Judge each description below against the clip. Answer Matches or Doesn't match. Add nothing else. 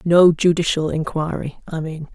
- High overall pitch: Doesn't match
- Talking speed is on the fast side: Doesn't match